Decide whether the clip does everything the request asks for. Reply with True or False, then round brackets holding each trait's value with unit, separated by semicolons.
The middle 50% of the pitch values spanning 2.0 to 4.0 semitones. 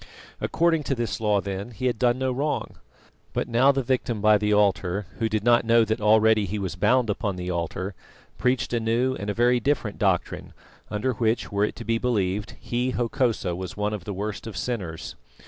True (3.2 semitones)